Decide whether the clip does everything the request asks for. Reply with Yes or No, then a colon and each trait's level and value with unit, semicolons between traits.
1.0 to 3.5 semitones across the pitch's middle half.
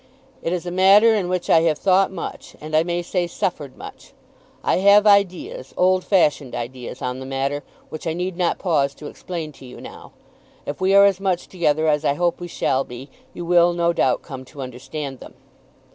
No: average, 4.3 semitones